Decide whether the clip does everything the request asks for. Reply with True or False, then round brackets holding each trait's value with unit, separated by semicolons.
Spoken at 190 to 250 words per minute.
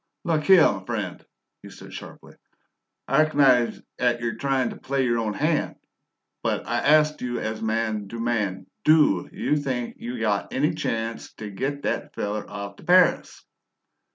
False (160 wpm)